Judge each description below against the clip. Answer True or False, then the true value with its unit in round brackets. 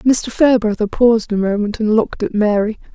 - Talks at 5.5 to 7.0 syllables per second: True (5.8 syllables/s)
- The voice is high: True (220 Hz)